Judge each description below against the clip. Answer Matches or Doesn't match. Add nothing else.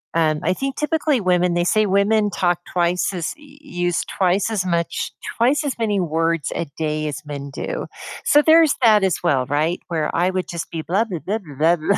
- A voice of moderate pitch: Matches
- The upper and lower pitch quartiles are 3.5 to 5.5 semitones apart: Matches